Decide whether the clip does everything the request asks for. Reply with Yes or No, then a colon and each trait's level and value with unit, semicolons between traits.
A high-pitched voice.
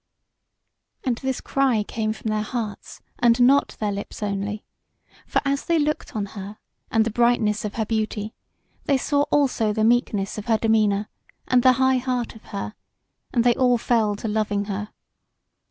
Yes: high, 220 Hz